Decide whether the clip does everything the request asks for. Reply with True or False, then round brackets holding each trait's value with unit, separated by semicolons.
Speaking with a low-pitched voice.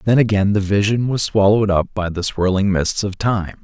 True (100 Hz)